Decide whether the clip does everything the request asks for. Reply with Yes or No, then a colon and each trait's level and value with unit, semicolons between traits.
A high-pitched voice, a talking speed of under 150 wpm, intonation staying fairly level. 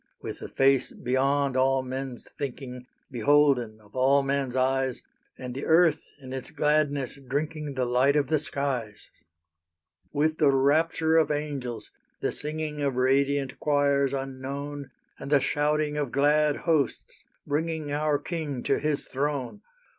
No: medium, 140 Hz; average, 140 wpm; narrow, 2.1 semitones